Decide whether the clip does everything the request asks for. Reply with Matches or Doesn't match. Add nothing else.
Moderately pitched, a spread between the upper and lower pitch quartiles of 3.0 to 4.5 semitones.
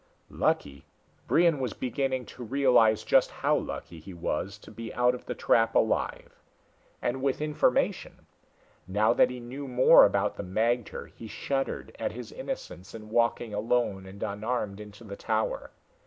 Doesn't match